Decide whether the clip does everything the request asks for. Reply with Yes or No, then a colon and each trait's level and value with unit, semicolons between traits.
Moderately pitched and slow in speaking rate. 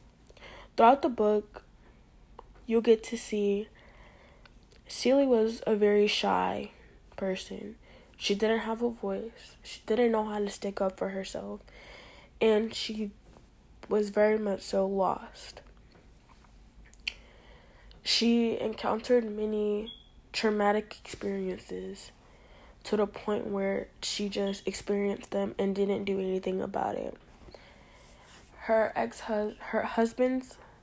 No: high, 210 Hz; slow, 110 wpm